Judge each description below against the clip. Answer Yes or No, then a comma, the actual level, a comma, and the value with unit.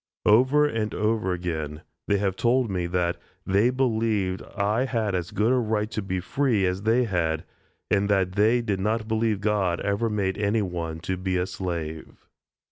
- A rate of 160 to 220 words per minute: Yes, average, 180 wpm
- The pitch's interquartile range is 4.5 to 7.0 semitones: No, average, 3.4 semitones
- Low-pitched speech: Yes, low, 100 Hz